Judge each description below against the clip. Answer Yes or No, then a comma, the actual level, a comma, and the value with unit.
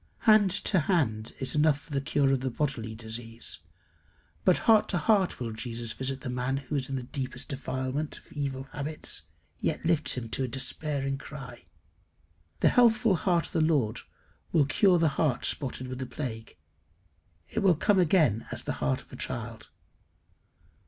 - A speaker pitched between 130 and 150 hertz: Yes, medium, 140 Hz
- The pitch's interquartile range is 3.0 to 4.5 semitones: Yes, average, 4.2 semitones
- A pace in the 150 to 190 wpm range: Yes, average, 170 wpm